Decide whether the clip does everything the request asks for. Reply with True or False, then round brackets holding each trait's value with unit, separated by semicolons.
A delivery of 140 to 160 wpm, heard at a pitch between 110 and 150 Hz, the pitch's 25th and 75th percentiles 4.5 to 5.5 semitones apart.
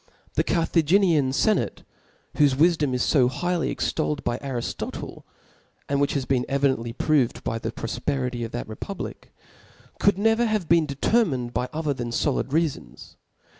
True (155 wpm; 140 Hz; 4.8 semitones)